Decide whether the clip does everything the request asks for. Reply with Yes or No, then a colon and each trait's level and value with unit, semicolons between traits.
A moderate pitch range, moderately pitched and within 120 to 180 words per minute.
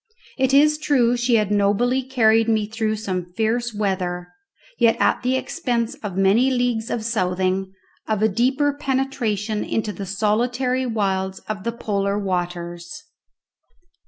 No: average, 4.0 semitones; high, 220 Hz; average, 140 wpm